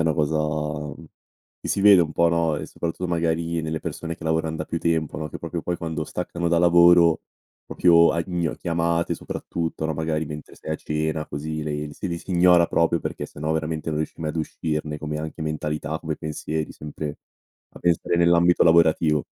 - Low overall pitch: Yes, very low, 80 Hz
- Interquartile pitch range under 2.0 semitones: Yes, narrow, 1.5 semitones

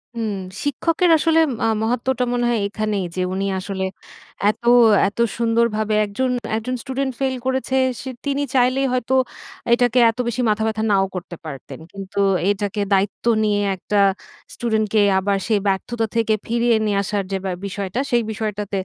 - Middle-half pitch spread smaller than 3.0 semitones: No, average, 3.6 semitones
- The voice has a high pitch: Yes, high, 220 Hz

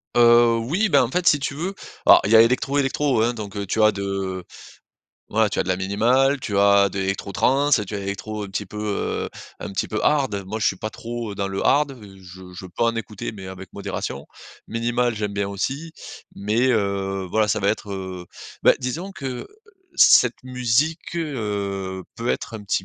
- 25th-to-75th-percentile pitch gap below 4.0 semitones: No, average, 4.3 semitones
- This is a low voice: Yes, low, 110 Hz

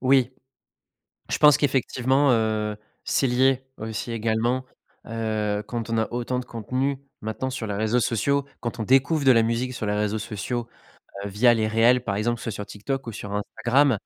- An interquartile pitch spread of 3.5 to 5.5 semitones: No, average, 3.0 semitones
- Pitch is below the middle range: Yes, low, 115 Hz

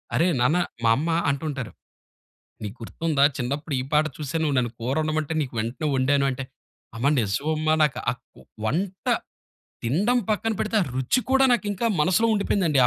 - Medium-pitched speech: Yes, medium, 150 Hz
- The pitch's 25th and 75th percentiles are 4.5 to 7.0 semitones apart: Yes, average, 5.2 semitones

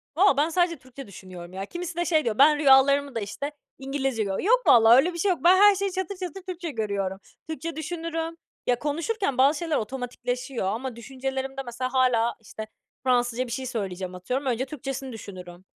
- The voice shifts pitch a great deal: Yes, wide, 5.9 semitones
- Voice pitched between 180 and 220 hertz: No, very high, 265 Hz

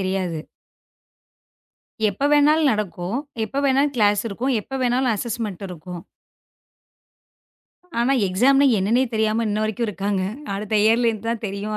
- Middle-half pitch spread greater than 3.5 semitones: Yes, average, 3.9 semitones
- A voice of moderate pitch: No, high, 215 Hz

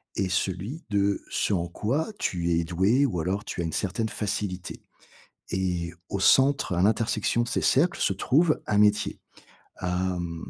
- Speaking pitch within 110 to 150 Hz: No, low, 100 Hz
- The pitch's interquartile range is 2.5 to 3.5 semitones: No, average, 3.9 semitones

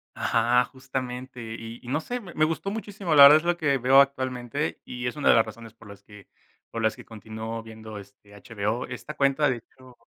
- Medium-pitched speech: No, low, 125 Hz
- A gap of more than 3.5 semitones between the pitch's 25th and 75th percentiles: Yes, average, 4.1 semitones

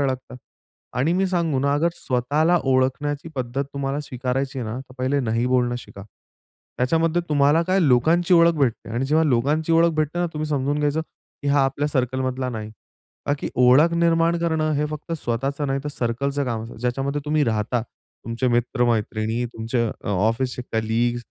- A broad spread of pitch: No, average, 3.9 semitones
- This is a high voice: No, low, 135 Hz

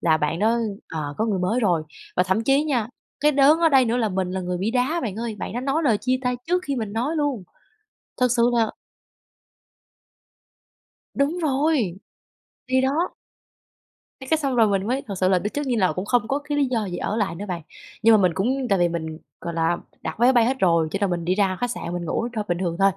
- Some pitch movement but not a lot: No, wide, 6.1 semitones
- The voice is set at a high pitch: Yes, high, 220 Hz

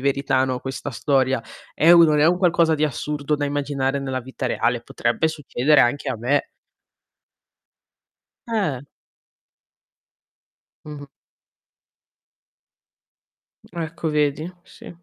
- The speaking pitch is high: No, medium, 145 Hz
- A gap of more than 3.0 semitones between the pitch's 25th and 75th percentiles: No, narrow, 2.6 semitones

